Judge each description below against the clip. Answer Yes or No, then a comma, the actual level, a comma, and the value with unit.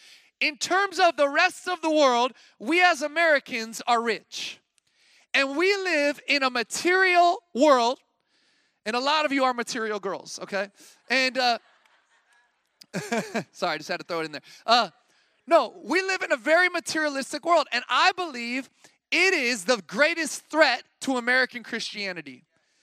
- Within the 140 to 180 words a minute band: Yes, average, 155 wpm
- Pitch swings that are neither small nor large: No, wide, 6.0 semitones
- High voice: Yes, very high, 280 Hz